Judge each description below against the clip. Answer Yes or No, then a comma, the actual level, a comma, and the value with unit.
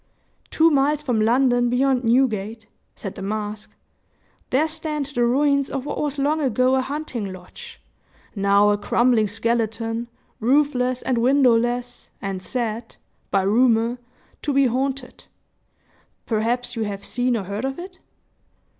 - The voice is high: Yes, high, 245 Hz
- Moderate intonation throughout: Yes, average, 3.6 semitones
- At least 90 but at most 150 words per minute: Yes, slow, 135 wpm